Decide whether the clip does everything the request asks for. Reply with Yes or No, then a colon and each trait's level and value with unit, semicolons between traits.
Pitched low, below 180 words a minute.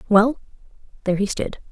No: high, 210 Hz; average, 140 wpm